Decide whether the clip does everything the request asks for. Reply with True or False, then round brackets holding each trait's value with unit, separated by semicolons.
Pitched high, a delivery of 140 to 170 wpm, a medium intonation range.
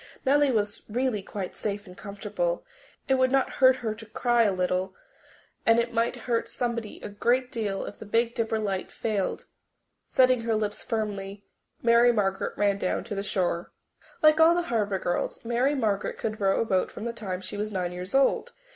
False (215 Hz; 190 wpm; 3.3 semitones)